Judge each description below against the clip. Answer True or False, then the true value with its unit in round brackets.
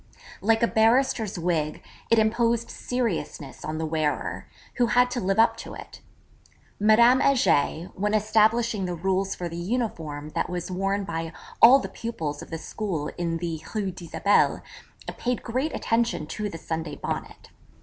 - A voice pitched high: True (200 Hz)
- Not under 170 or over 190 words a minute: False (160 wpm)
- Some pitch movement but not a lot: False (5.8 semitones)